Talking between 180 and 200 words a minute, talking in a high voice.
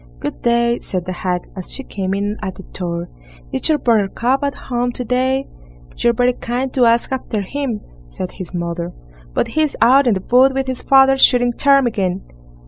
Yes: average, 190 wpm; high, 240 Hz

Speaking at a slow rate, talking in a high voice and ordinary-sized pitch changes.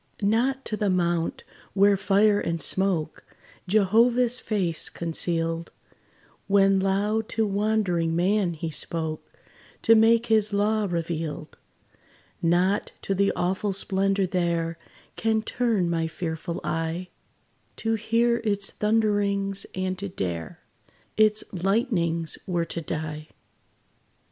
Yes: slow, 115 wpm; high, 195 Hz; average, 4.1 semitones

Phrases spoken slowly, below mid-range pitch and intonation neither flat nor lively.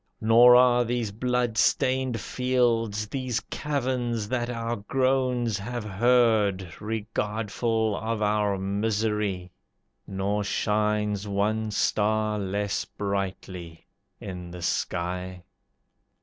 Yes: slow, 95 wpm; low, 110 Hz; average, 3.2 semitones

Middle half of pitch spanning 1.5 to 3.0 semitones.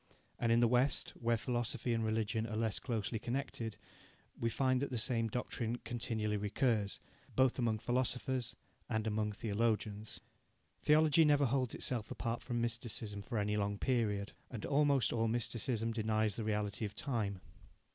Yes: narrow, 2.5 semitones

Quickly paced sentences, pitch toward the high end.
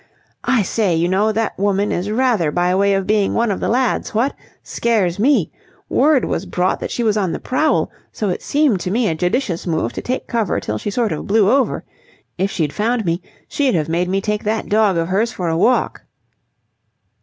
Yes: fast, 215 wpm; high, 205 Hz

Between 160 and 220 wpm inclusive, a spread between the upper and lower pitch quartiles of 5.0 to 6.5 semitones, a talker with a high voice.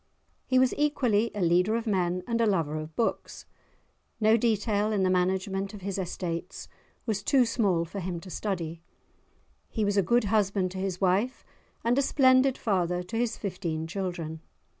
No: average, 175 wpm; average, 4.0 semitones; high, 195 Hz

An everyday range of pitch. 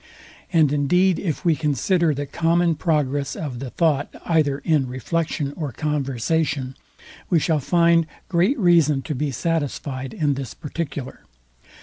Yes: average, 3.3 semitones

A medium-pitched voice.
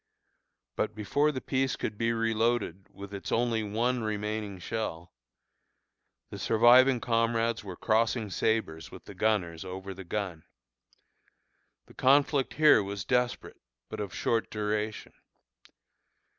No: low, 110 Hz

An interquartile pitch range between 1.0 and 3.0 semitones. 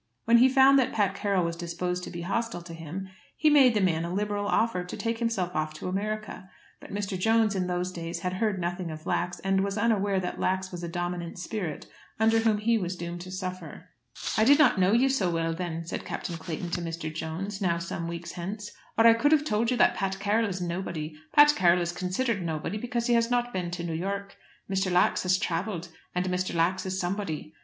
No: average, 3.7 semitones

